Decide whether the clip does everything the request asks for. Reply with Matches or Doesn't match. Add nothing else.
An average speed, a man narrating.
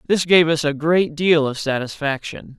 Matches